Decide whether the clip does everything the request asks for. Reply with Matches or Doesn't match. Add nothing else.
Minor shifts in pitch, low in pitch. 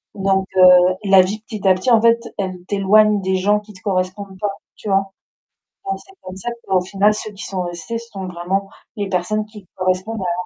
Doesn't match